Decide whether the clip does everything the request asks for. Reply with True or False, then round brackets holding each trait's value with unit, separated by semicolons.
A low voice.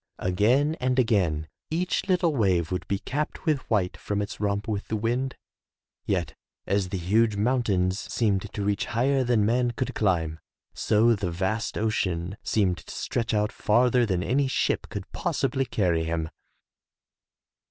True (105 Hz)